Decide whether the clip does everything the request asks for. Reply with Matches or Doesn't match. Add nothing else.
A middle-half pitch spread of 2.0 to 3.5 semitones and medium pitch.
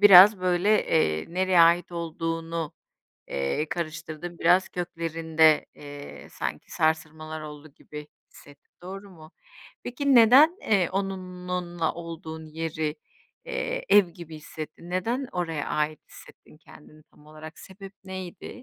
Matches